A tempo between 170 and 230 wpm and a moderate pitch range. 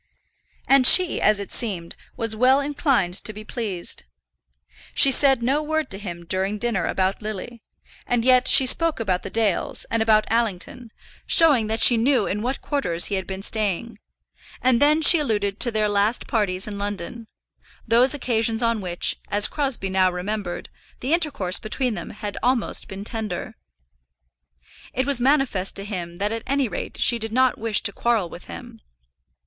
Yes: average, 175 wpm; average, 4.3 semitones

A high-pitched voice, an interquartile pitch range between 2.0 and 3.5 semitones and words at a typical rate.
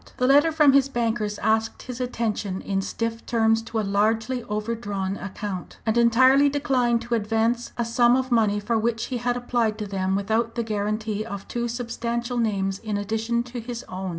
Yes: high, 230 Hz; narrow, 2.4 semitones; average, 185 wpm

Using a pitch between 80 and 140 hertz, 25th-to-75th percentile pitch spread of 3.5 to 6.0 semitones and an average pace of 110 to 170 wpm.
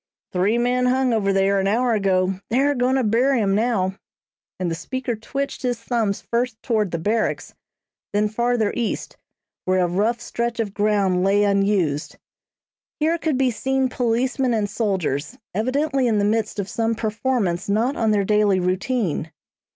No: high, 220 Hz; average, 3.9 semitones; average, 165 wpm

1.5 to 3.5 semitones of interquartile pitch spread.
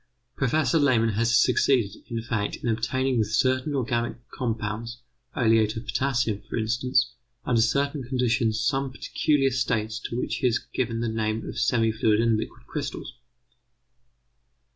Yes: narrow, 2.6 semitones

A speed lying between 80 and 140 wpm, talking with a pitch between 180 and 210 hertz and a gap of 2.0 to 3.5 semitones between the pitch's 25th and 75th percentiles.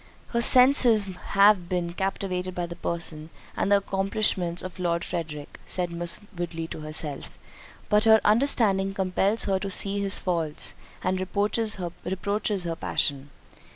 Yes: slow, 135 wpm; medium, 185 Hz; average, 2.9 semitones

